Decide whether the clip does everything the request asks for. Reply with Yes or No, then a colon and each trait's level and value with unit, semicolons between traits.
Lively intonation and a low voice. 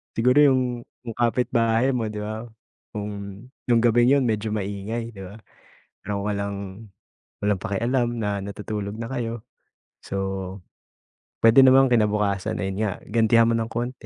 No: narrow, 2.5 semitones; low, 110 Hz